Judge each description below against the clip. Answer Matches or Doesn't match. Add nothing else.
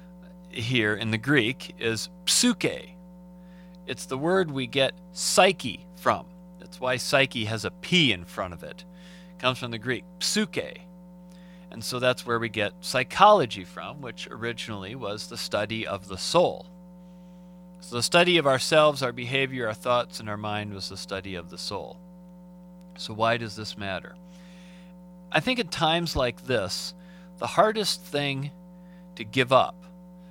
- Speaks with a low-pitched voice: Doesn't match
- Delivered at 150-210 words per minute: Matches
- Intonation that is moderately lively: Doesn't match